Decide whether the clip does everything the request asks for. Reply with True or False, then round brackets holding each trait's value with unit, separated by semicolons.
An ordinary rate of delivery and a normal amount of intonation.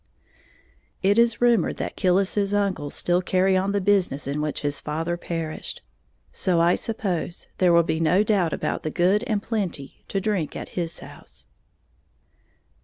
True (160 wpm; 3.5 semitones)